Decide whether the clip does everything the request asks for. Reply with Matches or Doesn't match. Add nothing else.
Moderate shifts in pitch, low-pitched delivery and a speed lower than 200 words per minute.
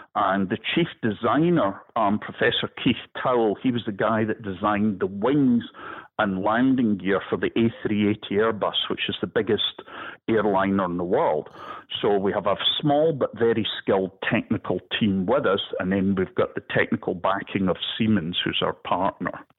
Matches